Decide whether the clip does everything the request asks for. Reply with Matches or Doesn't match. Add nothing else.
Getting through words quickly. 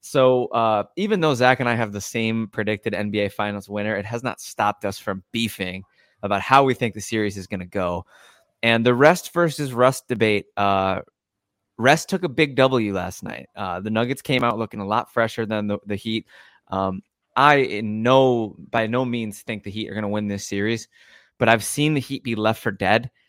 Matches